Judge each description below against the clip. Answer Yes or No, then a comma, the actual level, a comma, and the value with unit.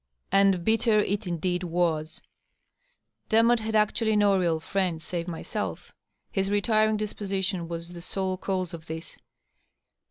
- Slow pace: Yes, slow, 130 wpm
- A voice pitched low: No, high, 190 Hz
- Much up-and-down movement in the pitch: No, average, 3.7 semitones